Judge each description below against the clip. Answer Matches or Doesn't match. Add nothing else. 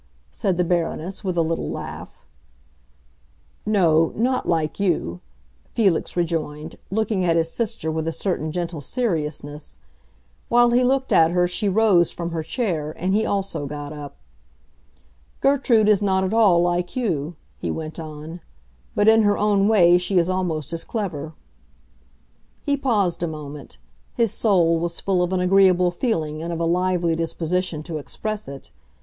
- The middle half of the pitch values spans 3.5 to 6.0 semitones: Matches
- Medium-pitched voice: Matches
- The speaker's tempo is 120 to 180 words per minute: Matches